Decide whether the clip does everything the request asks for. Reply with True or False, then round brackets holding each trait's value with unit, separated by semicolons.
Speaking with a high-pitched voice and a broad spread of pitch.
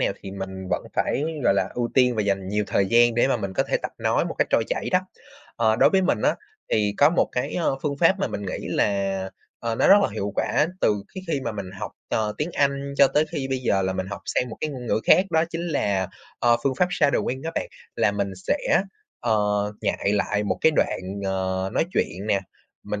False (115 Hz; 6.0 semitones)